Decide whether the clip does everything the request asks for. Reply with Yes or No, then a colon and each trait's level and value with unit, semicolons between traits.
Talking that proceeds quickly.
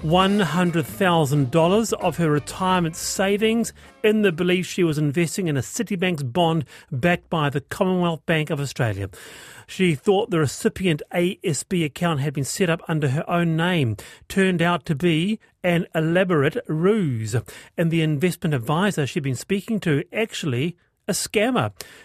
No: average, 145 wpm